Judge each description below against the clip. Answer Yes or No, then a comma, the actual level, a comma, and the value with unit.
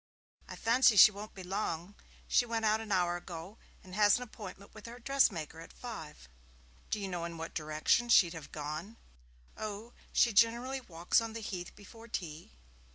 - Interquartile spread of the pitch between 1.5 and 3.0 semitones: No, average, 5.1 semitones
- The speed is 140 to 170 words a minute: No, average, 185 wpm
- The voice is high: Yes, high, 205 Hz